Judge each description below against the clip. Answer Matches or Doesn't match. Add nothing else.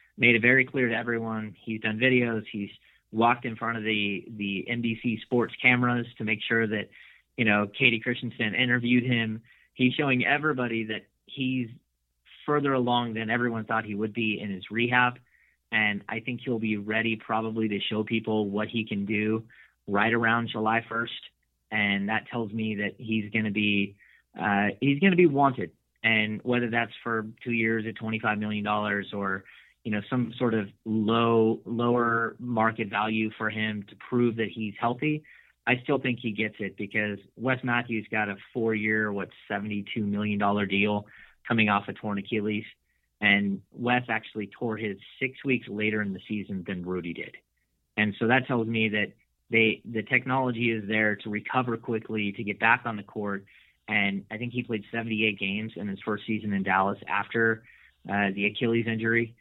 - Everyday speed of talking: Matches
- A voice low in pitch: Matches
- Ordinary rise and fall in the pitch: Doesn't match